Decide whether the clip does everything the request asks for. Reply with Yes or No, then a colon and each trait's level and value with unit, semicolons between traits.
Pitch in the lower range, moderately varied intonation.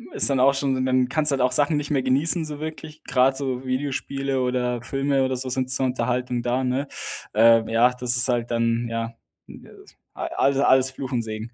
No: low, 130 Hz; narrow, 1.9 semitones